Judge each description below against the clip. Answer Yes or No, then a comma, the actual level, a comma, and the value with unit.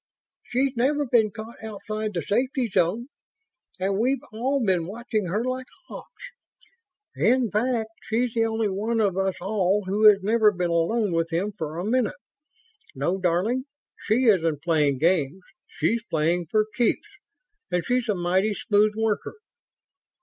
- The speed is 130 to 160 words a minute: Yes, average, 150 wpm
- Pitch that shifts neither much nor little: Yes, average, 4.5 semitones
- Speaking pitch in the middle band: No, high, 210 Hz